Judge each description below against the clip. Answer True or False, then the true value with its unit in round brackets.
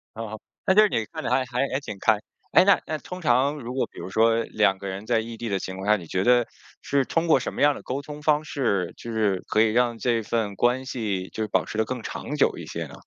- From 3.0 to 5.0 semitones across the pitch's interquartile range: True (4.3 semitones)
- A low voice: True (115 Hz)